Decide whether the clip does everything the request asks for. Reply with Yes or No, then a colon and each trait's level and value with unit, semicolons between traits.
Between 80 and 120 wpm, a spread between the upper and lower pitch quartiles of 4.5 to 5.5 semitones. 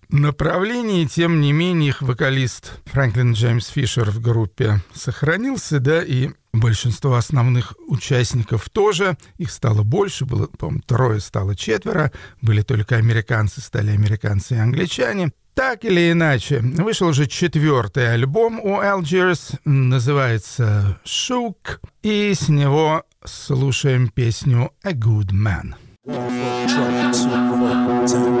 Yes: slow, 110 wpm; average, 5.1 semitones